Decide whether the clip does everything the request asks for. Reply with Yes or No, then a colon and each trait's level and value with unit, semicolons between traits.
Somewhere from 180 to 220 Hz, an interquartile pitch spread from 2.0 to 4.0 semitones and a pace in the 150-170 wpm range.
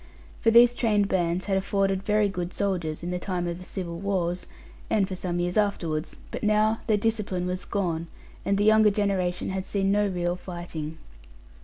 No: high, 190 Hz; average, 2.7 semitones; average, 185 wpm